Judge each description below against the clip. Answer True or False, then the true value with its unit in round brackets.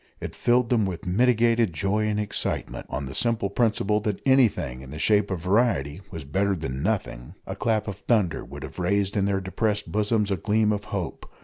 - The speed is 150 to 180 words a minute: False (200 wpm)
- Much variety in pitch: False (3.3 semitones)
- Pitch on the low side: True (100 Hz)